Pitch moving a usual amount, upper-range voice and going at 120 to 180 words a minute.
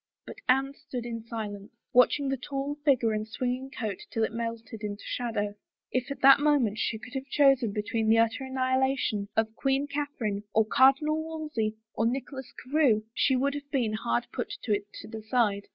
No: average, 3.8 semitones; high, 245 Hz; average, 195 wpm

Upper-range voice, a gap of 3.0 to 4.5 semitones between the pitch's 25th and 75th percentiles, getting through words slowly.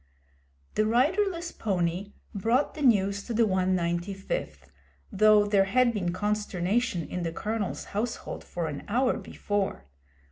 Yes: high, 205 Hz; average, 4.1 semitones; slow, 130 wpm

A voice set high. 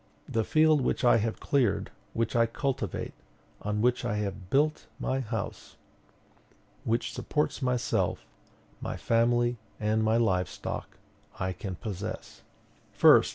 No: low, 115 Hz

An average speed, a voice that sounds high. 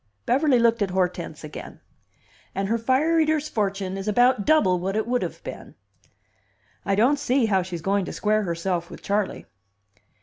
Yes: average, 170 wpm; high, 210 Hz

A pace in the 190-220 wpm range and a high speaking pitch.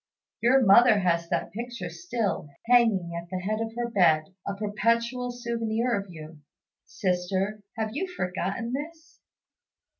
No: average, 140 wpm; high, 215 Hz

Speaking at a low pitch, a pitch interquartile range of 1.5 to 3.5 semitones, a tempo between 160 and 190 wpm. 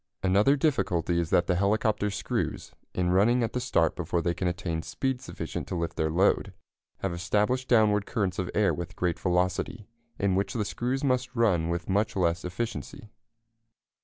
No: very low, 95 Hz; average, 4.6 semitones; average, 175 wpm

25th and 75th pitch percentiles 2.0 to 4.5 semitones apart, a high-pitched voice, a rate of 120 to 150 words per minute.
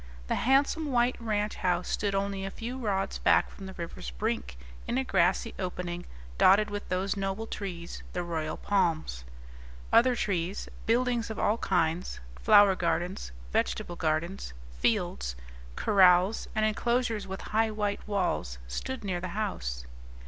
Yes: average, 3.9 semitones; high, 195 Hz; average, 145 wpm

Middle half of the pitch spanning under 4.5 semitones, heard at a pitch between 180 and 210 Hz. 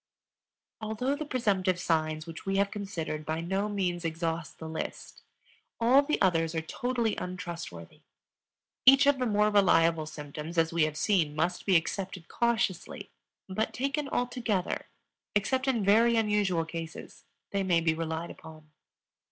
No: average, 5.0 semitones; medium, 185 Hz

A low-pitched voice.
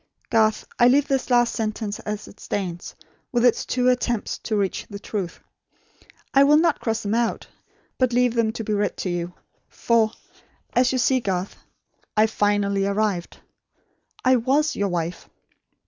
No: high, 220 Hz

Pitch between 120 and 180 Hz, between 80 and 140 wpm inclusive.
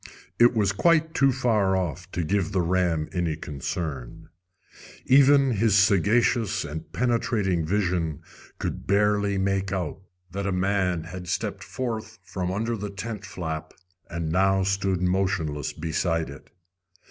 No: very low, 95 Hz; slow, 135 wpm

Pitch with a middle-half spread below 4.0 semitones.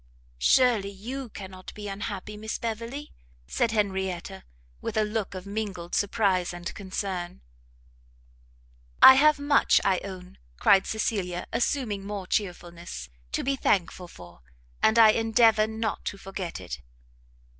Yes: average, 3.2 semitones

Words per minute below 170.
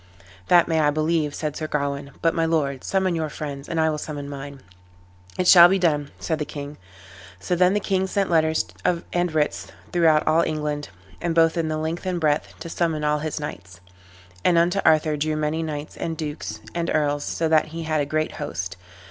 No: average, 200 wpm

